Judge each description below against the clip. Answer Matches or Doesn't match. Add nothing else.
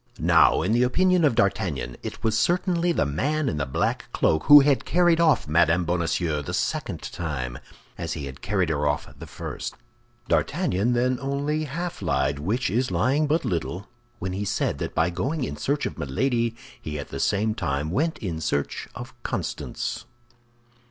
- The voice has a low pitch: Matches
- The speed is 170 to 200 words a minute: Matches